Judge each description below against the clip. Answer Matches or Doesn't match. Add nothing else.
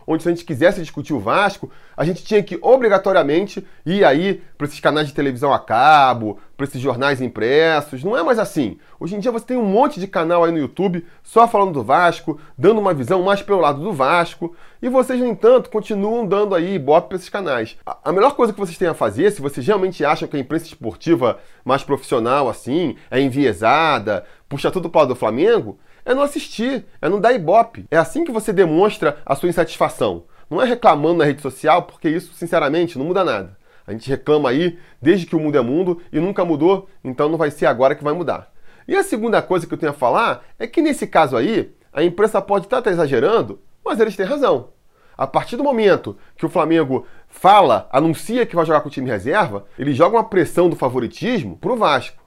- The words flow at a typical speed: Doesn't match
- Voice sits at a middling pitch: Matches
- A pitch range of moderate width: Doesn't match